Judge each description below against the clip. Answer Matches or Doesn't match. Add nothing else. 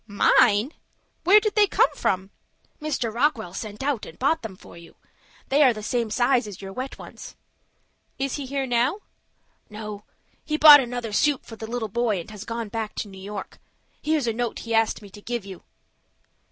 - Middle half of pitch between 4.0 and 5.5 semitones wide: Matches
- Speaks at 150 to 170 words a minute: Doesn't match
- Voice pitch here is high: Matches